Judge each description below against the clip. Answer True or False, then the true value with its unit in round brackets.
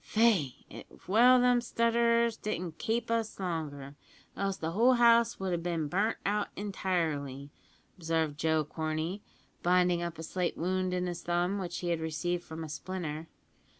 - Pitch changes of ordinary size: True (4.7 semitones)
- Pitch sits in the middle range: True (180 Hz)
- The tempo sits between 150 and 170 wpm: True (160 wpm)